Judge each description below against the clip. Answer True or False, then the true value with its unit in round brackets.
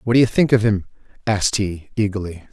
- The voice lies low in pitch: True (105 Hz)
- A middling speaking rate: False (215 wpm)